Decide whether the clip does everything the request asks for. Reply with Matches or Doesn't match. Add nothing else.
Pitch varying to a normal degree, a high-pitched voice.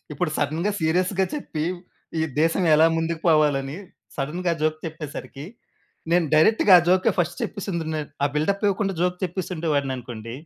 Doesn't match